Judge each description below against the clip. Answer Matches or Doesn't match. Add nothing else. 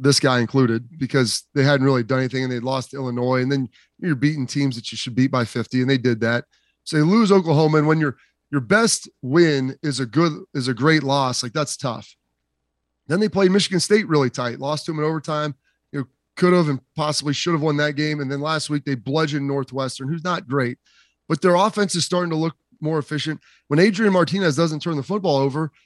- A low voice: Doesn't match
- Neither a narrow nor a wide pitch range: Matches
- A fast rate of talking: Matches